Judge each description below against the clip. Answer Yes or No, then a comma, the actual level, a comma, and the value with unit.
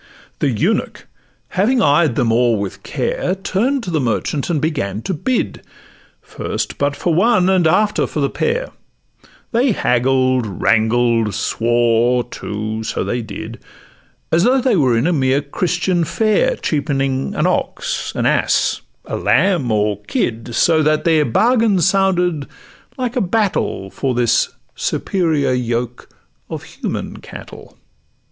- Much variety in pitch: Yes, wide, 7.8 semitones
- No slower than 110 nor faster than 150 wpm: Yes, average, 140 wpm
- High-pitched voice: No, medium, 145 Hz